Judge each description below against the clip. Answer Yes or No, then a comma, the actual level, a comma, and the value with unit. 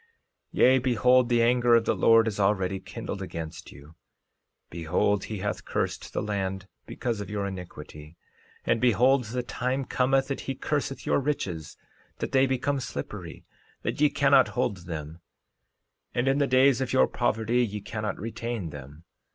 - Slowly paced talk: No, average, 165 wpm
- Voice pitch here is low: Yes, low, 115 Hz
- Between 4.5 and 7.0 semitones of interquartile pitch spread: Yes, average, 5.1 semitones